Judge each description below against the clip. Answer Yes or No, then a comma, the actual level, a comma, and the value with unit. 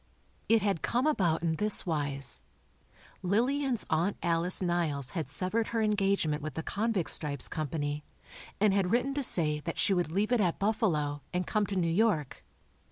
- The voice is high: No, medium, 180 Hz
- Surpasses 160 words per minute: Yes, average, 170 wpm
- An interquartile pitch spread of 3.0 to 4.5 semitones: No, wide, 5.4 semitones